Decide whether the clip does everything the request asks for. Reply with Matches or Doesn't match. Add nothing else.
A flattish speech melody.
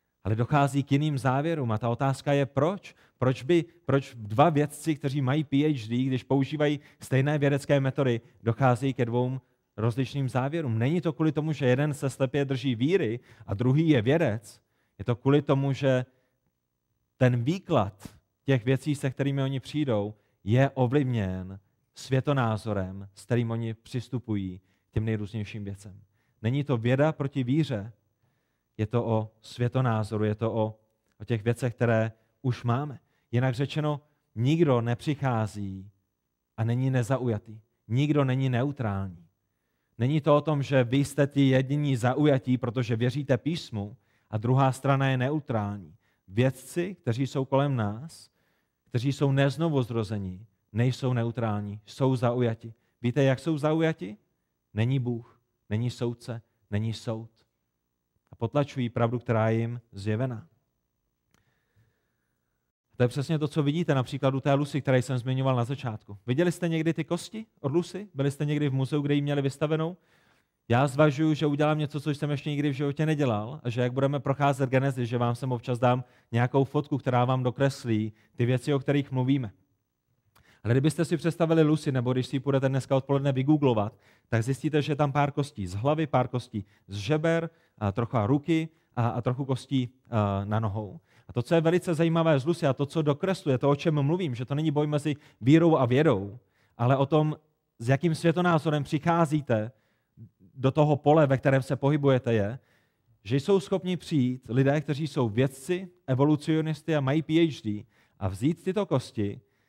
Doesn't match